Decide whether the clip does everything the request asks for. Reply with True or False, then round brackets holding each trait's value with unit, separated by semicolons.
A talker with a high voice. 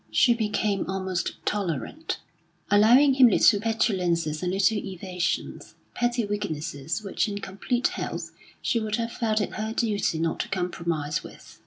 True (205 Hz)